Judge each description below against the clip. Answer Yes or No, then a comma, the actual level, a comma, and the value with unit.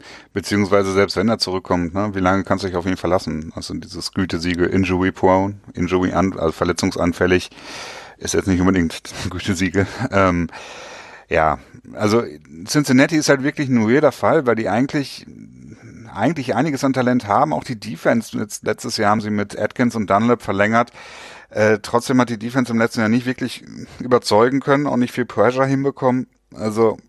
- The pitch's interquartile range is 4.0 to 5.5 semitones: Yes, average, 4.7 semitones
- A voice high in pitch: No, low, 105 Hz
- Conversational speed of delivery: Yes, average, 170 wpm